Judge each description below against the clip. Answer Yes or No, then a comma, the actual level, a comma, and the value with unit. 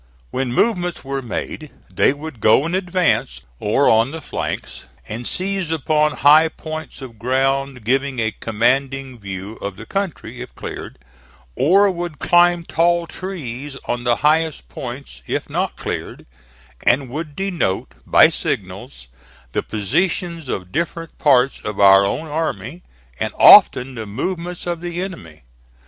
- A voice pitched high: No, medium, 140 Hz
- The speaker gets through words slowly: No, average, 145 wpm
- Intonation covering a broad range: Yes, wide, 6.2 semitones